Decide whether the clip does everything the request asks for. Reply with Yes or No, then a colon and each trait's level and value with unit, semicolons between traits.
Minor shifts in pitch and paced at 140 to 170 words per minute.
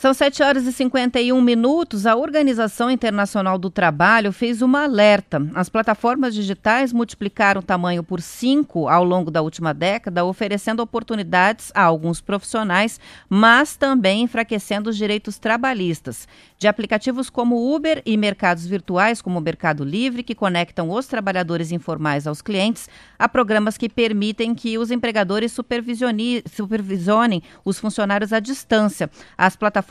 No: average, 4.1 semitones; average, 145 wpm